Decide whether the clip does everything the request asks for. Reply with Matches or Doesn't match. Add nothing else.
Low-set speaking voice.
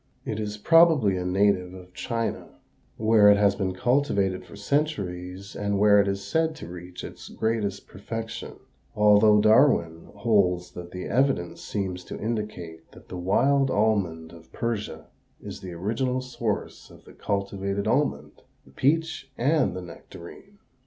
Matches